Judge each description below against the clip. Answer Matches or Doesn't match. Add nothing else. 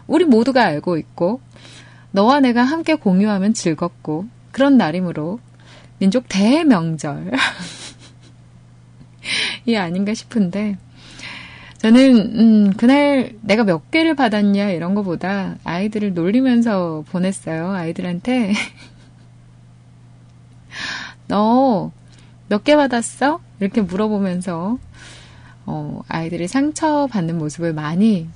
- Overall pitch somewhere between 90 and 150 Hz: Doesn't match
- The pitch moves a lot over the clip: Matches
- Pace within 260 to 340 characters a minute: Doesn't match